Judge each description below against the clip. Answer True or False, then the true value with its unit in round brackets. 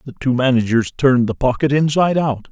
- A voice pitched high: False (135 Hz)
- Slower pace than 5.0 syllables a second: False (6.1 syllables/s)